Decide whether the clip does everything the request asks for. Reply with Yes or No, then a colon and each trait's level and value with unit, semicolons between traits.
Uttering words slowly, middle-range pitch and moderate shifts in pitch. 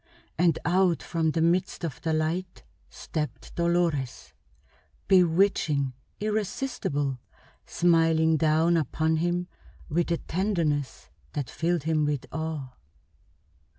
No: slow, 105 wpm; medium, 165 Hz; narrow, 2.3 semitones